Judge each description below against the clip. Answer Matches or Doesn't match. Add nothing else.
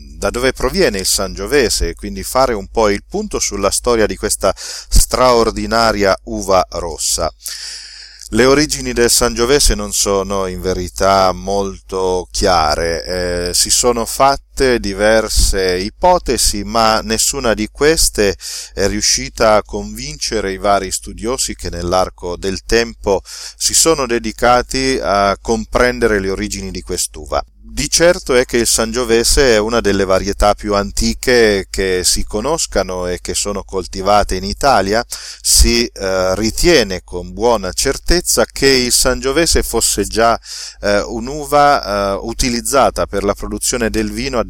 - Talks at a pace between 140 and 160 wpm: Doesn't match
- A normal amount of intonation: Matches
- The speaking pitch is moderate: Doesn't match